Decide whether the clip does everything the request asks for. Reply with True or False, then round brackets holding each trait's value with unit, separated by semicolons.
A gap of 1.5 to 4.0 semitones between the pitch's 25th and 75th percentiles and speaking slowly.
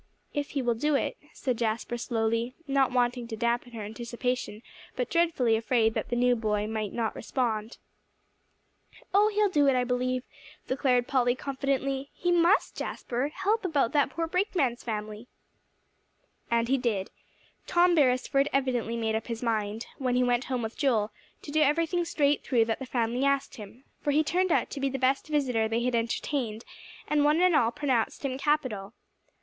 False (3.7 semitones; 180 wpm)